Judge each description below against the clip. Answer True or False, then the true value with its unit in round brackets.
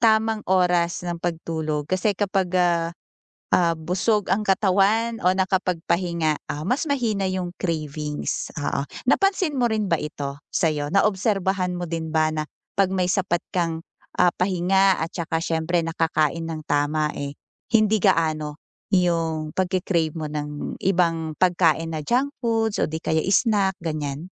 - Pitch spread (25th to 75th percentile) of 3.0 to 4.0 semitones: True (3.4 semitones)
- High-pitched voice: False (175 Hz)